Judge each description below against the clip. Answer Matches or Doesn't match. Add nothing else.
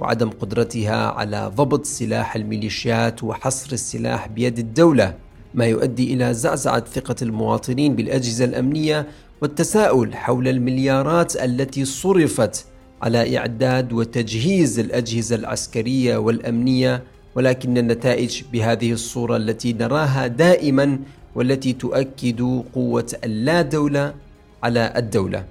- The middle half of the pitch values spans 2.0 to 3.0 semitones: Matches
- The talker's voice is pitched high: Doesn't match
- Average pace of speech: Matches